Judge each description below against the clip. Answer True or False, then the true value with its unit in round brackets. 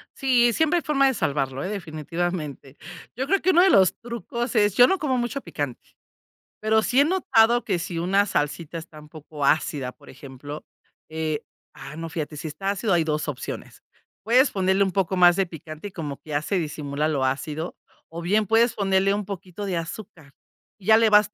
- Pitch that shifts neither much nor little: False (6.3 semitones)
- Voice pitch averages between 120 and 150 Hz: False (180 Hz)